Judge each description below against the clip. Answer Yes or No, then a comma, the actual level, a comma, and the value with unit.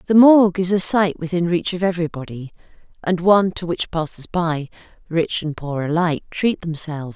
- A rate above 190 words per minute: No, average, 175 wpm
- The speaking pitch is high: No, medium, 170 Hz